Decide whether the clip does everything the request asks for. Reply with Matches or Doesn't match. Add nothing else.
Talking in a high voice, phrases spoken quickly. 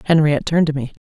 Doesn't match